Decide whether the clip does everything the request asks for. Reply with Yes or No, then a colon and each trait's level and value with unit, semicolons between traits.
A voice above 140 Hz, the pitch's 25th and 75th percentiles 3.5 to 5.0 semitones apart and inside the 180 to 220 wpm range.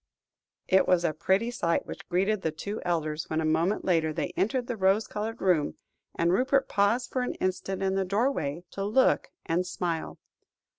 Yes: high, 190 Hz; average, 4.2 semitones; average, 185 wpm